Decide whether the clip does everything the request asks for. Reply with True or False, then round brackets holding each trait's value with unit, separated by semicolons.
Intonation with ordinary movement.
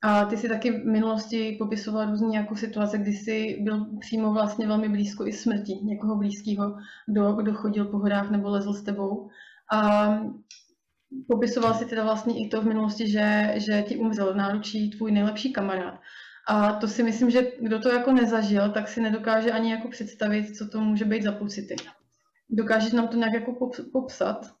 False (1.4 semitones)